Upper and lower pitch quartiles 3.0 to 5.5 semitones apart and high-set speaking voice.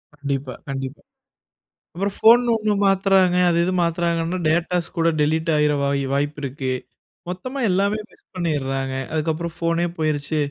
No: average, 3.9 semitones; medium, 165 Hz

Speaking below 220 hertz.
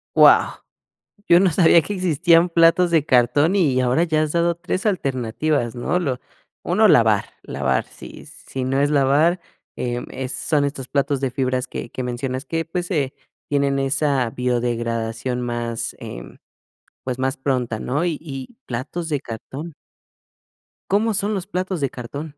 Yes: medium, 140 Hz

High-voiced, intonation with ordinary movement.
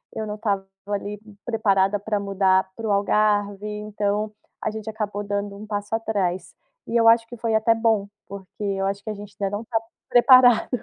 No: high, 210 Hz; narrow, 1.7 semitones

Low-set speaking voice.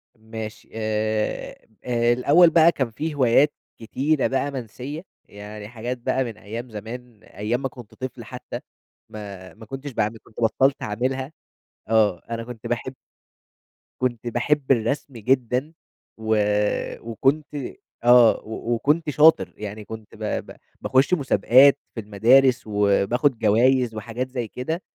Yes: low, 120 Hz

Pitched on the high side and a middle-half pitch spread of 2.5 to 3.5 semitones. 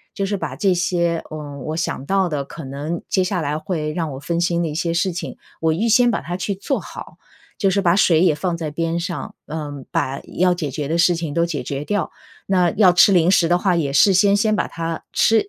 No: medium, 170 Hz; average, 3.2 semitones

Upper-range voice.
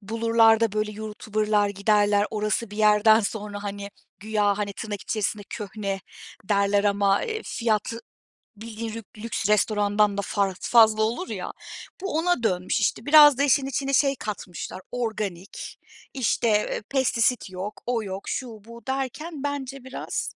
Yes: high, 215 Hz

